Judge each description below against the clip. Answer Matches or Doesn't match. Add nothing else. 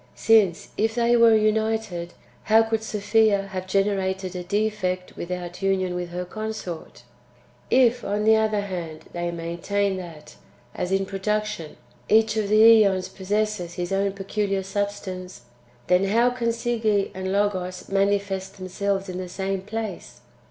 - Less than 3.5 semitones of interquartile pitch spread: Matches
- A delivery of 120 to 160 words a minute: Matches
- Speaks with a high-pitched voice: Matches